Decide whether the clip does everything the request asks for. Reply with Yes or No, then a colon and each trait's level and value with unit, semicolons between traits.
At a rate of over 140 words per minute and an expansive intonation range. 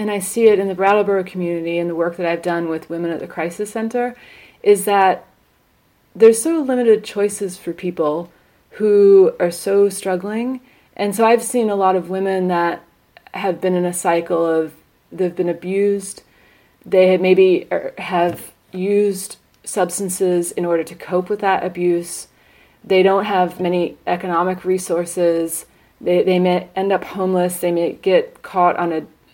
No: average, 170 wpm; narrow, 2.5 semitones